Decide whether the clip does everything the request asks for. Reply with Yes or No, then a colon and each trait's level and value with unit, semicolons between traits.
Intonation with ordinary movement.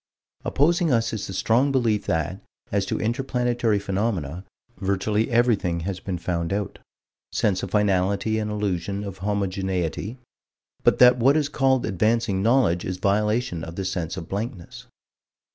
Yes: average, 3.9 semitones